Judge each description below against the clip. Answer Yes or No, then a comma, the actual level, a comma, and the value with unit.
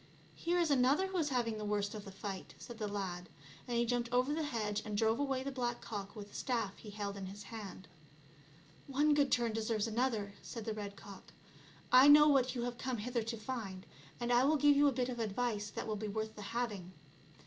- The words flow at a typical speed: No, fast, 240 wpm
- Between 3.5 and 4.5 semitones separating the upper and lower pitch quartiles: Yes, average, 3.8 semitones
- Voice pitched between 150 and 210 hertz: No, high, 230 Hz